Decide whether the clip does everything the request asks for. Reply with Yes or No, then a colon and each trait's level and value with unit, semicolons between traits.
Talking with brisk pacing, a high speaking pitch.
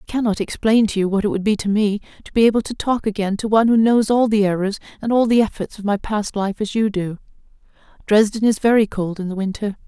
Yes: fast, 255 wpm; high, 210 Hz